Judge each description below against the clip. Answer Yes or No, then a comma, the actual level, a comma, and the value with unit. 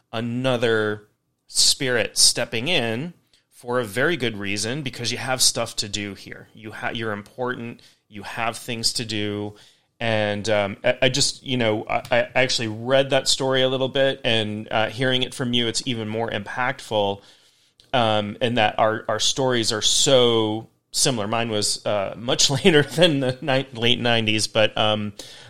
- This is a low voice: Yes, low, 115 Hz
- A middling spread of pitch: Yes, average, 3.2 semitones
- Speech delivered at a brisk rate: No, average, 170 wpm